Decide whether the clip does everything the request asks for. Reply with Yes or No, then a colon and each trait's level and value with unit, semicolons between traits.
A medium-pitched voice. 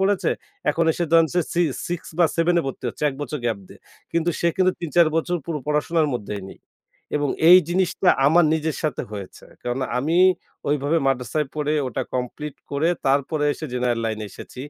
Yes: medium, 150 Hz